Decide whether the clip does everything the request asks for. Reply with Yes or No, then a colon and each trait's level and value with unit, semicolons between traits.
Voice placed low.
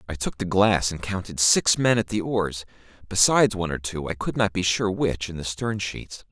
Yes: very low, 95 Hz